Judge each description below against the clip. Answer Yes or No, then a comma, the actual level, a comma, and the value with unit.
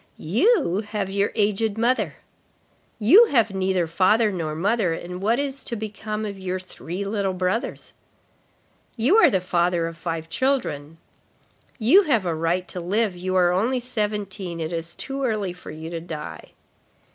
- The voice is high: Yes, high, 195 Hz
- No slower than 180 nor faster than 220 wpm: No, average, 155 wpm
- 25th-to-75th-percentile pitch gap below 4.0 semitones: No, average, 4.3 semitones